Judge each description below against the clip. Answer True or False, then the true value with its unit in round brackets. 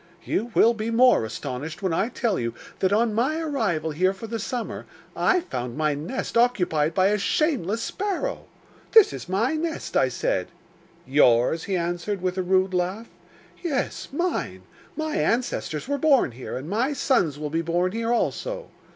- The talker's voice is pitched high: True (205 Hz)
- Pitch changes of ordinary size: False (7.7 semitones)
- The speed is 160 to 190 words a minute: True (170 wpm)